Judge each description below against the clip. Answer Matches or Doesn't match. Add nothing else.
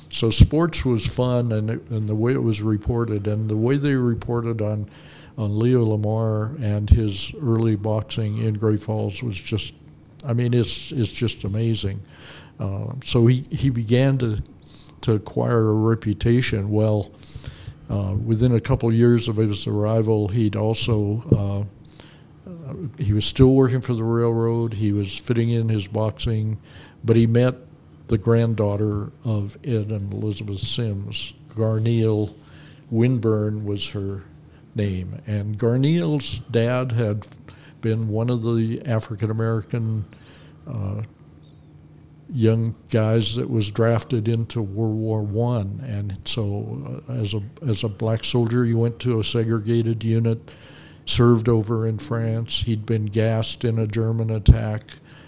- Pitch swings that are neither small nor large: Doesn't match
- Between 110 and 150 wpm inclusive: Matches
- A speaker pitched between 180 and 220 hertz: Doesn't match